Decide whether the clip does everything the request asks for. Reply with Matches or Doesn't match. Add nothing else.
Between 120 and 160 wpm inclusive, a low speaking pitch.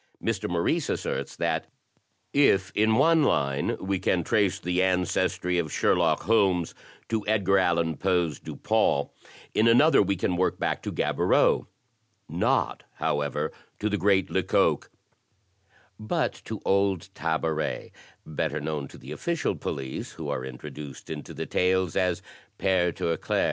Matches